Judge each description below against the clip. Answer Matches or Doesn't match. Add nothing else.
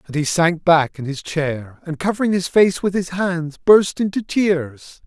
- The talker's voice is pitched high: Doesn't match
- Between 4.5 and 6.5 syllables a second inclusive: Doesn't match